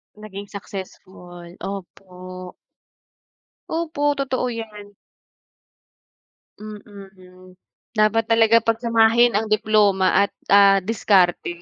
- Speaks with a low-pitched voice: No, high, 205 Hz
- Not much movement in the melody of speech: No, average, 3.1 semitones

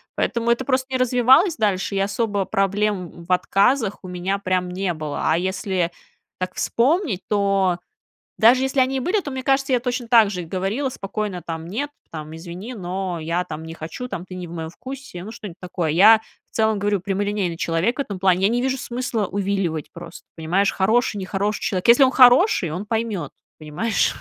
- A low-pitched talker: No, high, 200 Hz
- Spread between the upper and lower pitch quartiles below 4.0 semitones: No, average, 4.9 semitones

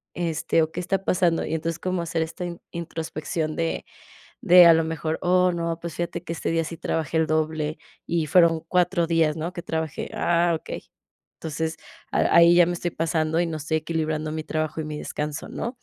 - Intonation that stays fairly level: Yes, narrow, 1.5 semitones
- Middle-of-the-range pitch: Yes, medium, 165 Hz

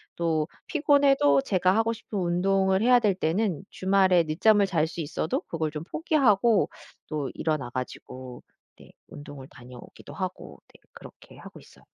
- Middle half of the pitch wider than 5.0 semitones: Yes, wide, 5.5 semitones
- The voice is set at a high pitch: No, medium, 180 Hz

